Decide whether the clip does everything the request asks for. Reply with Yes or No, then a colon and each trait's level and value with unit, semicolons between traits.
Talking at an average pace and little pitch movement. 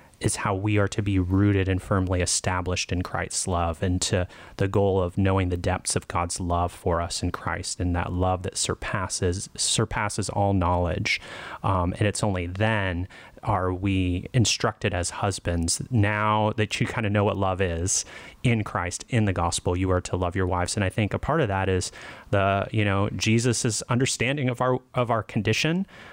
No: average, 195 wpm; average, 3.2 semitones